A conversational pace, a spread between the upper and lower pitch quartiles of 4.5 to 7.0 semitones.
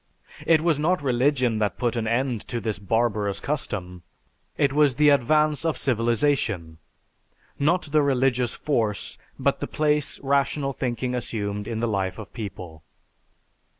Yes: average, 145 wpm; average, 5.1 semitones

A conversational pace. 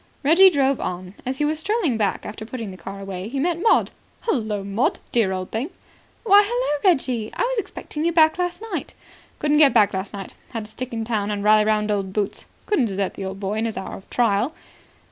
No: fast, 220 wpm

